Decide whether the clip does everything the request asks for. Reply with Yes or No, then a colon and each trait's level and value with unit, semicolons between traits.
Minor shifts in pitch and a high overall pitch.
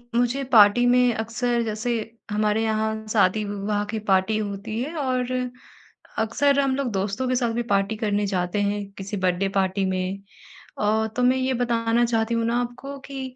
No: average, 3.2 semitones; high, 220 Hz